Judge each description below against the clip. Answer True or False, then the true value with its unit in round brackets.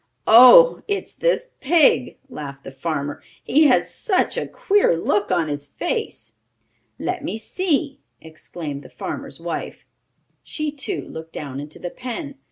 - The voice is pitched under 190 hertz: False (245 Hz)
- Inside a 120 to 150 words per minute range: True (145 wpm)